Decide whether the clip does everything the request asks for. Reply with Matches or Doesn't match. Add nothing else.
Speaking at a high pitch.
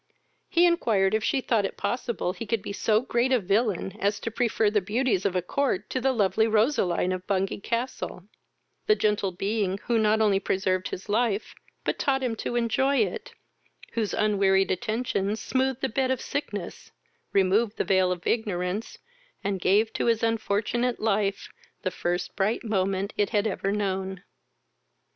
Matches